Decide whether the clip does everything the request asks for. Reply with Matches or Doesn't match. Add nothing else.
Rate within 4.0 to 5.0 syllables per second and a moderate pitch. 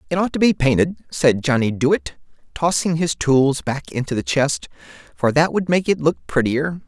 Matches